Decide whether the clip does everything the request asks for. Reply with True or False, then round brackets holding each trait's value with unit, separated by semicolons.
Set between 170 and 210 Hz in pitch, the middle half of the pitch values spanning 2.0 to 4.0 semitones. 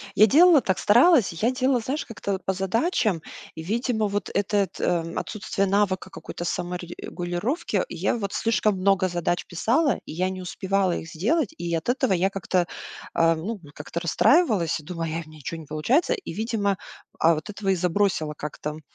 False (190 Hz; 4.5 semitones)